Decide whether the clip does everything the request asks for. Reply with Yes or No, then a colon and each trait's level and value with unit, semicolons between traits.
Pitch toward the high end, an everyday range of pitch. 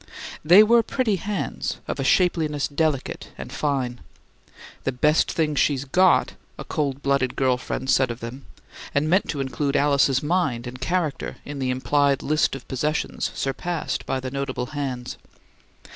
No: medium, 140 Hz; average, 3.0 semitones